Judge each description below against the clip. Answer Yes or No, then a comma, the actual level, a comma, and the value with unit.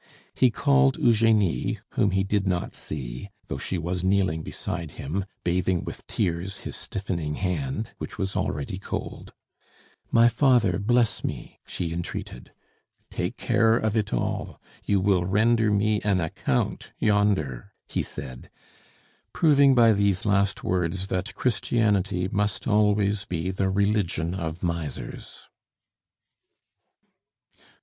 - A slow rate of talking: Yes, slow, 125 wpm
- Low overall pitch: Yes, very low, 95 Hz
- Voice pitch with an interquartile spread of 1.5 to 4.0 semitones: Yes, average, 3.5 semitones